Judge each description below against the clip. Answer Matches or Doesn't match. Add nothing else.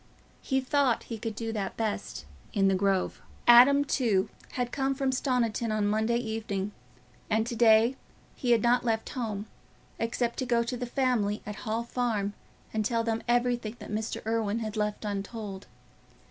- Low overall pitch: Doesn't match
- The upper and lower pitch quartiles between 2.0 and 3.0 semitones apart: Matches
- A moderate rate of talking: Matches